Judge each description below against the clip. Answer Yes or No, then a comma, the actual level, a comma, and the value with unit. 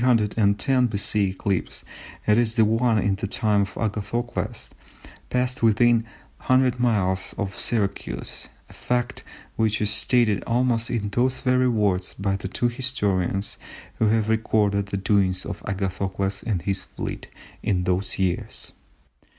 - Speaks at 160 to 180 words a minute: No, slow, 135 wpm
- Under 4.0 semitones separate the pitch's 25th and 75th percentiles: Yes, average, 3.4 semitones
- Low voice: Yes, low, 105 Hz